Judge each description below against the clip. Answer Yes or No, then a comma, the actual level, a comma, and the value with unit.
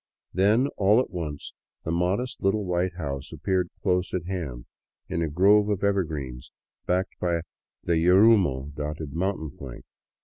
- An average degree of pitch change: Yes, average, 4.2 semitones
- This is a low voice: Yes, very low, 90 Hz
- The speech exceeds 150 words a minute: No, average, 145 wpm